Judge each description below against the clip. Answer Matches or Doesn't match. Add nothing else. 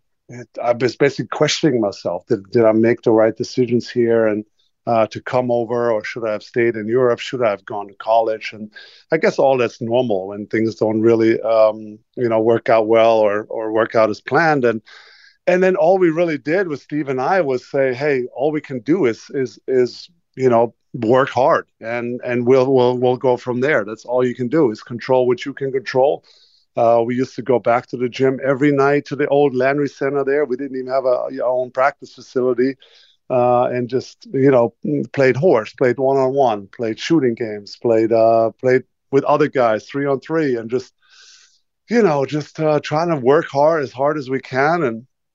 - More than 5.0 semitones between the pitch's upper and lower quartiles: Doesn't match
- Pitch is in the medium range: Doesn't match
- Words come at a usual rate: Doesn't match